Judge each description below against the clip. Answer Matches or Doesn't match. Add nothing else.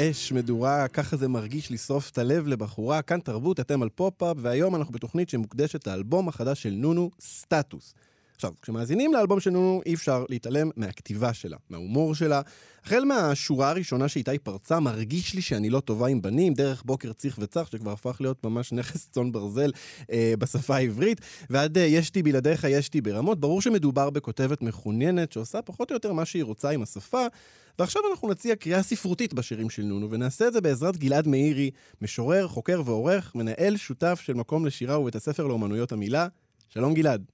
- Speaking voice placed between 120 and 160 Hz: Matches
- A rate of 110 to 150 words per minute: Doesn't match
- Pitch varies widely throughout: Matches